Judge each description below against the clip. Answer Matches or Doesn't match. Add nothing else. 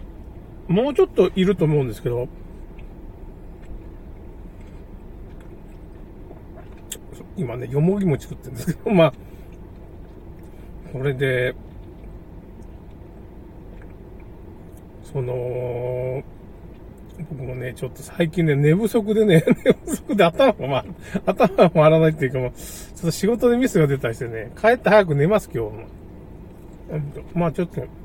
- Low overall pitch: Matches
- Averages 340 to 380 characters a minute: Doesn't match